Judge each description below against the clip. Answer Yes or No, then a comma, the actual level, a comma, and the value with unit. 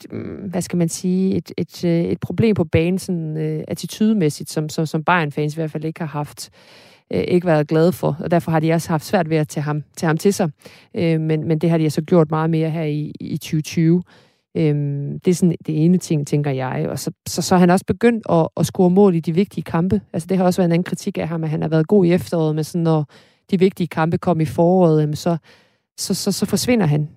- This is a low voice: No, medium, 165 Hz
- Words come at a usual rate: No, fast, 255 wpm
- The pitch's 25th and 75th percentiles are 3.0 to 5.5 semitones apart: No, narrow, 2.5 semitones